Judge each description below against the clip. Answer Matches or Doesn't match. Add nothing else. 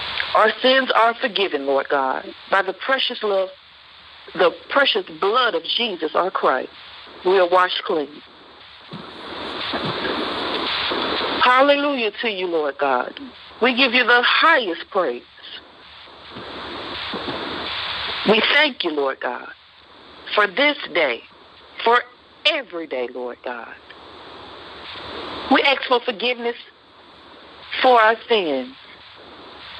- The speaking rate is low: Matches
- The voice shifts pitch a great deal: Matches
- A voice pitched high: Matches